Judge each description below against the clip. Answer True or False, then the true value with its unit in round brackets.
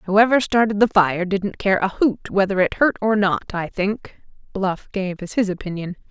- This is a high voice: True (200 Hz)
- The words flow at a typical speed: True (195 wpm)